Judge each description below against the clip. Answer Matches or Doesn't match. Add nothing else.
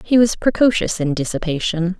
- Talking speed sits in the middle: Matches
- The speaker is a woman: Matches